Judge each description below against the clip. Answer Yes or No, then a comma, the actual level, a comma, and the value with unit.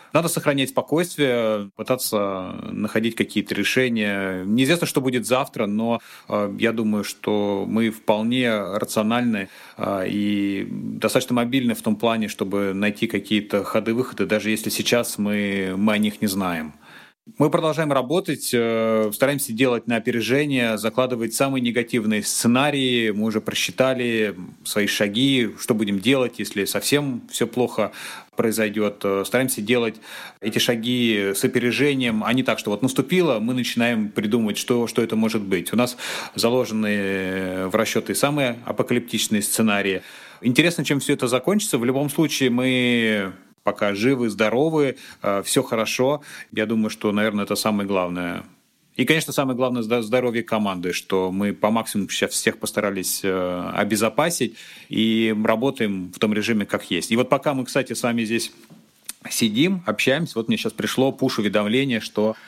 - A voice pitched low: Yes, low, 115 Hz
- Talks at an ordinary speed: Yes, average, 140 wpm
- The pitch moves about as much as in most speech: Yes, average, 3.5 semitones